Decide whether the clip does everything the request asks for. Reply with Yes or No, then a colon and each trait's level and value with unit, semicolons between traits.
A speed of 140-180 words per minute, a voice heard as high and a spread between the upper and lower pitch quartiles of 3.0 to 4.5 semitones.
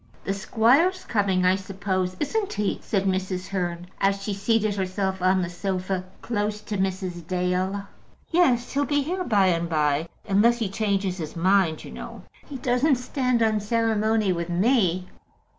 Yes: average, 160 wpm; high, 195 Hz; average, 3.6 semitones